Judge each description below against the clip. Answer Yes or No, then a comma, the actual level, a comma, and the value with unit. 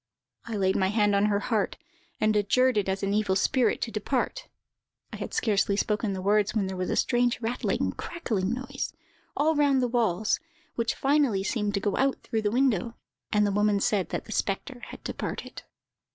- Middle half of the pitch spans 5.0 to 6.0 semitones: No, average, 3.5 semitones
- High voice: Yes, high, 215 Hz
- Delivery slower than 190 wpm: No, average, 195 wpm